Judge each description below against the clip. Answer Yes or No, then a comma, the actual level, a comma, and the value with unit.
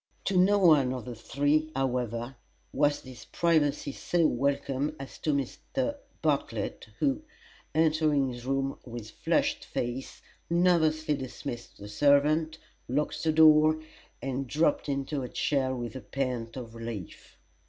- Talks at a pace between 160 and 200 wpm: No, slow, 135 wpm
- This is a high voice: No, medium, 140 Hz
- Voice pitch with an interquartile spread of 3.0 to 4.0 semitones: Yes, average, 3.7 semitones